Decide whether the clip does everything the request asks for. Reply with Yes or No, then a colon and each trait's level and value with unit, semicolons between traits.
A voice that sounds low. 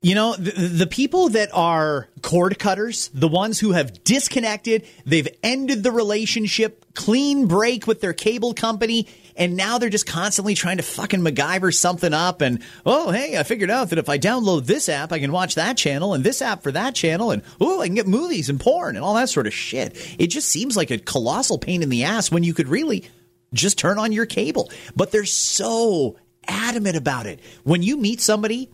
No: high, 200 Hz